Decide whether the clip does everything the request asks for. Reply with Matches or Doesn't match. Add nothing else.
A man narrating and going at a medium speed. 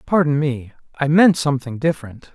Matches